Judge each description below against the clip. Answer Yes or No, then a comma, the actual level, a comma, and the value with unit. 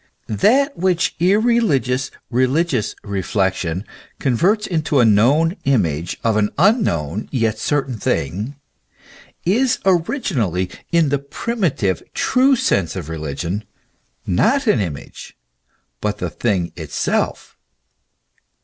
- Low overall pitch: Yes, low, 125 Hz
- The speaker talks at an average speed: No, slow, 105 wpm